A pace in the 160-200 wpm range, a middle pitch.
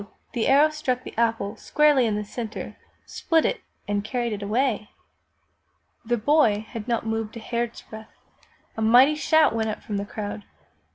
No: average, 165 wpm; high, 230 Hz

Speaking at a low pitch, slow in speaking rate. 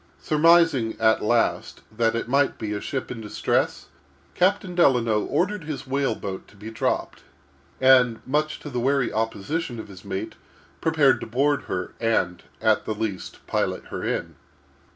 No: low, 125 Hz; average, 160 wpm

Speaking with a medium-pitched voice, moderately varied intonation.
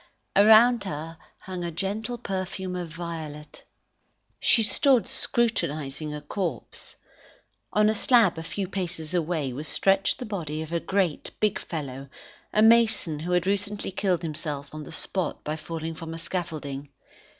Yes: medium, 175 Hz; average, 4.6 semitones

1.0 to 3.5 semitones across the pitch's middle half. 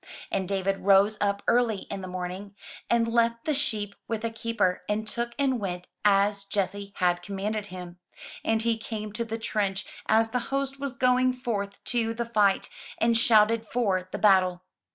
Yes: average, 2.9 semitones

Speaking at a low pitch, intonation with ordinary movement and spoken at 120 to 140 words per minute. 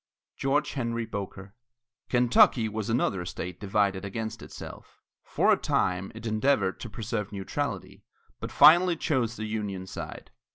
Yes: low, 110 Hz; average, 3.5 semitones; slow, 135 wpm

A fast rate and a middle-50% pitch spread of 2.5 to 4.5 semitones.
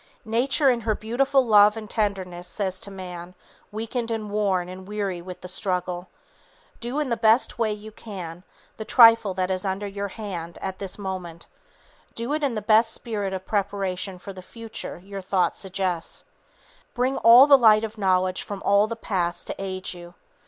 No: average, 180 wpm; average, 3.2 semitones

